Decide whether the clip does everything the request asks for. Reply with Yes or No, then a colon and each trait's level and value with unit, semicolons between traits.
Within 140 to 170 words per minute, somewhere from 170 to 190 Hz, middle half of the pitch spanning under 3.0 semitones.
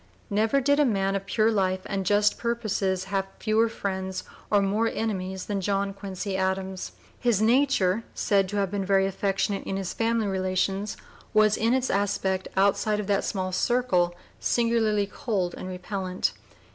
No: average, 160 wpm; high, 200 Hz; narrow, 2.4 semitones